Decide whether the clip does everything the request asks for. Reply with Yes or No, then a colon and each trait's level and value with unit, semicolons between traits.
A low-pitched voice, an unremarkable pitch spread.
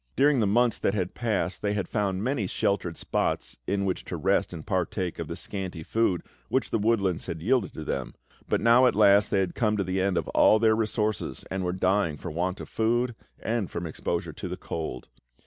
Yes: low, 100 Hz; average, 3.6 semitones